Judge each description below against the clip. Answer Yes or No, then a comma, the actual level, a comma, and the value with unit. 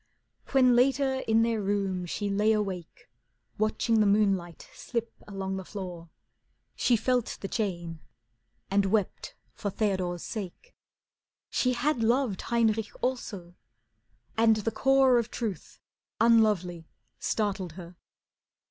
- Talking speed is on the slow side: Yes, slow, 120 wpm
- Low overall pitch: No, high, 210 Hz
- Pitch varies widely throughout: No, average, 3.6 semitones